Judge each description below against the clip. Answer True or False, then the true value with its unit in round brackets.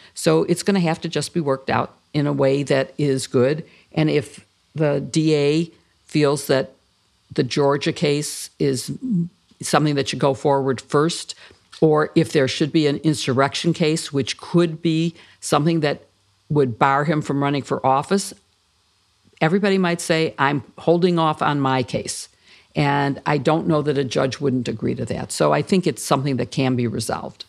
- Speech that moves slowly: False (175 wpm)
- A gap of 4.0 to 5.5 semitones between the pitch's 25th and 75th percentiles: False (3.1 semitones)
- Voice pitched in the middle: True (145 Hz)